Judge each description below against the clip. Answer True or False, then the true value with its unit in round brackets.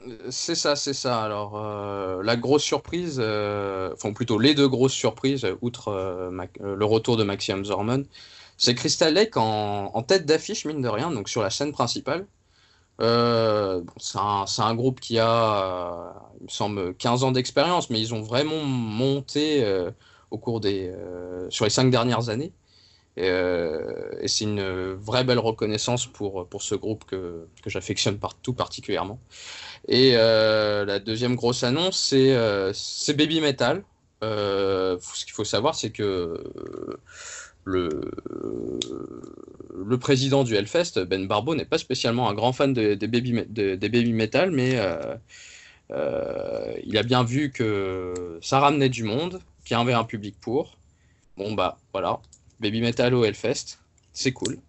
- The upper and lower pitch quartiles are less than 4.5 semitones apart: False (5.6 semitones)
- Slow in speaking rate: False (170 wpm)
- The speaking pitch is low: True (115 Hz)